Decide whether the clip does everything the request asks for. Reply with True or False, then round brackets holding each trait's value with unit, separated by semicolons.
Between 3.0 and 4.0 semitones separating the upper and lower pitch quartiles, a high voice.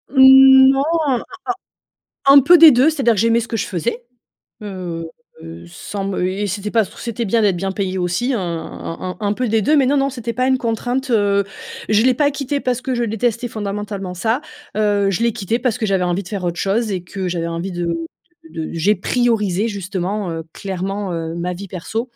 False (4.6 semitones; 210 Hz)